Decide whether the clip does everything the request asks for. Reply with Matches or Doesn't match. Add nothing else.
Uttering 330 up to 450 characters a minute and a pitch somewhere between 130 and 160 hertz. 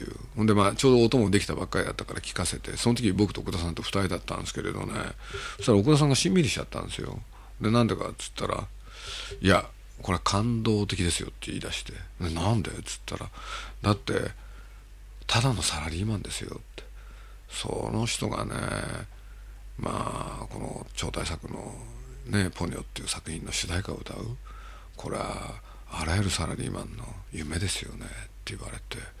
Doesn't match